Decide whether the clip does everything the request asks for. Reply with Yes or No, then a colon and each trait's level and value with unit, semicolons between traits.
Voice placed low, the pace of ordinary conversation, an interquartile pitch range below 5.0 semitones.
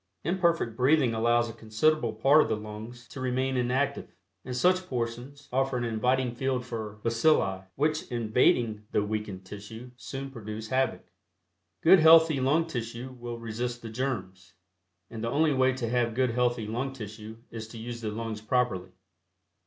Yes: low, 120 Hz; average, 160 wpm; average, 3.2 semitones